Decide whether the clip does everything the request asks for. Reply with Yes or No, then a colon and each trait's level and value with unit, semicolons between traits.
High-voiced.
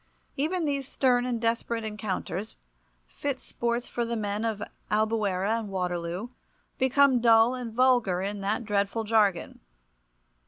Yes: high, 225 Hz